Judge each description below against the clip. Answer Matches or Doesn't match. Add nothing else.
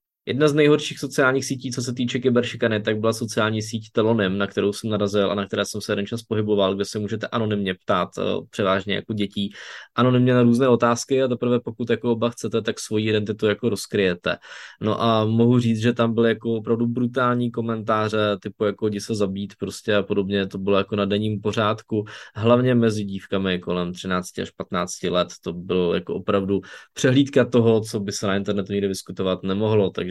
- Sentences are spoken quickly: Matches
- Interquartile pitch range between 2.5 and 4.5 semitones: Matches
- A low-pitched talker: Matches